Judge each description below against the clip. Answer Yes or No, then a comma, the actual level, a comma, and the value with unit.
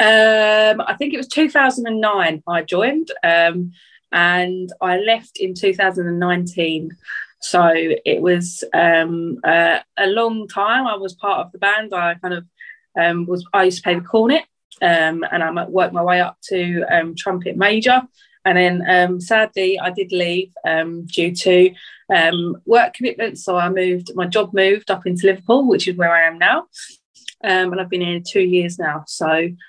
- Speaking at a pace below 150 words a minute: No, average, 175 wpm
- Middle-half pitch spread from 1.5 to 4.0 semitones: Yes, average, 3.3 semitones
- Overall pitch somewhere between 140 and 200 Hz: Yes, medium, 185 Hz